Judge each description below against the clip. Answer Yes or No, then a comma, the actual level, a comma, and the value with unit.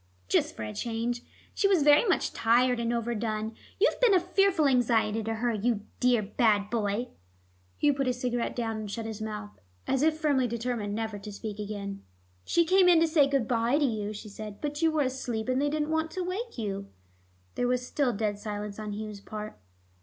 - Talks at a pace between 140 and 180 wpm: No, fast, 205 wpm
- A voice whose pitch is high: Yes, high, 235 Hz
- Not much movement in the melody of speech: No, average, 5.2 semitones